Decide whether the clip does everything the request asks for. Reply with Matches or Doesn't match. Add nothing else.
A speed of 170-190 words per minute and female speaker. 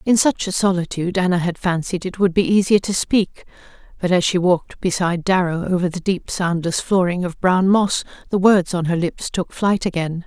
Doesn't match